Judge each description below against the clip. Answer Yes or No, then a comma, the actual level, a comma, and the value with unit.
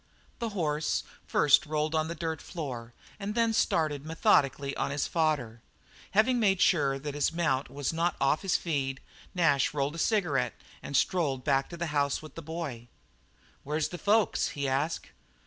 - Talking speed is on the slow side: No, average, 170 wpm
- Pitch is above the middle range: No, medium, 155 Hz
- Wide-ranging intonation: No, average, 3.5 semitones